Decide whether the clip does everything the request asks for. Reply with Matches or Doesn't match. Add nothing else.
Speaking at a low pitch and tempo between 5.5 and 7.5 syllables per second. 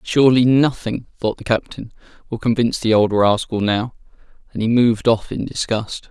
Doesn't match